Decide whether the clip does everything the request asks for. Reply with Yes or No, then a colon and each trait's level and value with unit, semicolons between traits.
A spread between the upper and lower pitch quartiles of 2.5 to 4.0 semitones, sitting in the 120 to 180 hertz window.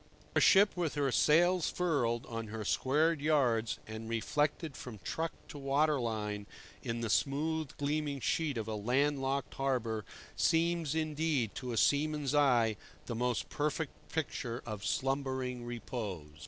No: average, 4.7 semitones; low, 135 Hz